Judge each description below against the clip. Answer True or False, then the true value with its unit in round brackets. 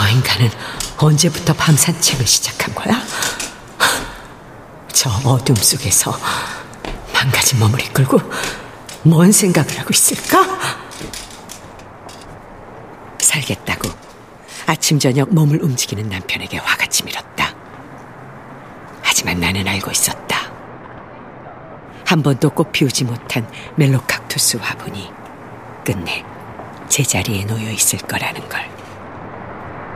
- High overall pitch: False (135 Hz)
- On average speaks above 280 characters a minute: False (210 characters per minute)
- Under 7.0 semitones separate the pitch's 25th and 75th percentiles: True (5.6 semitones)